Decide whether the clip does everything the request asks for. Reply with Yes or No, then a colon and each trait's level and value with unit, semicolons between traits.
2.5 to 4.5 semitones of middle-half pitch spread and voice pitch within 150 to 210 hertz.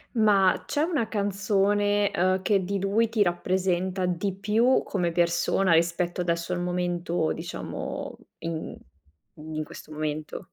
Yes: average, 2.9 semitones; medium, 185 Hz